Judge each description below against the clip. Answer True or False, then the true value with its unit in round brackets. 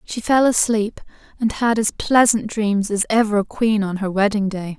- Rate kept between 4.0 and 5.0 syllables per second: True (4.6 syllables/s)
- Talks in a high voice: True (215 Hz)